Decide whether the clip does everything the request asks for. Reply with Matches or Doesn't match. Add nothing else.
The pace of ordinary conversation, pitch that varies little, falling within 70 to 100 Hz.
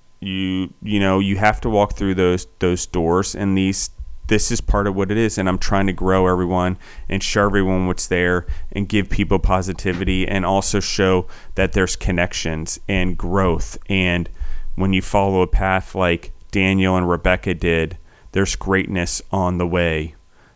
Matches